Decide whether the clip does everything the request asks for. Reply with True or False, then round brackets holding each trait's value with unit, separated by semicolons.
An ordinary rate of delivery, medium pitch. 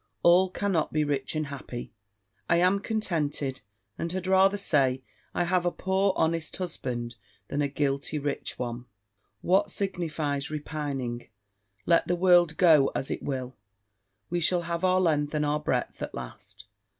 True (155 wpm; 155 Hz)